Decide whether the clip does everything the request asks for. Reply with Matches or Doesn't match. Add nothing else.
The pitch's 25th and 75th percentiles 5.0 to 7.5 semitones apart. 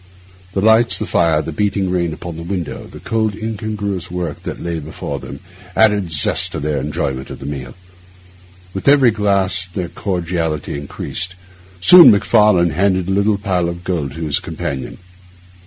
Doesn't match